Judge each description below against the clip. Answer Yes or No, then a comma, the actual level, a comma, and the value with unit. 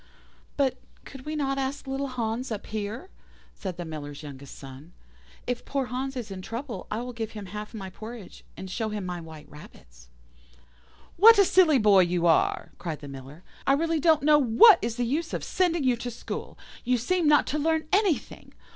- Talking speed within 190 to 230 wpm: Yes, average, 195 wpm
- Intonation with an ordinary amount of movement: No, wide, 7.5 semitones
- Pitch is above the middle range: Yes, high, 235 Hz